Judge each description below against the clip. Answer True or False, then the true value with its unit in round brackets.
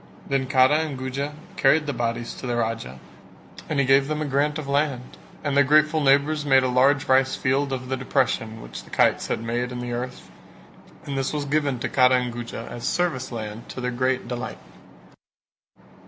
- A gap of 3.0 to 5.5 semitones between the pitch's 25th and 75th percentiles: False (2.6 semitones)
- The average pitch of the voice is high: False (130 Hz)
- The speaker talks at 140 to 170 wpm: False (200 wpm)